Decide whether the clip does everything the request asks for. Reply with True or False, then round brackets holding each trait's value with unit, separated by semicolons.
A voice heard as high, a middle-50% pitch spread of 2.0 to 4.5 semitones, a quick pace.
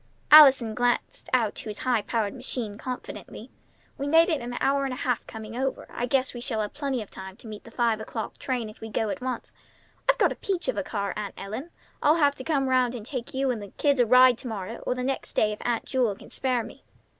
True (245 Hz; 3.5 semitones; 255 wpm)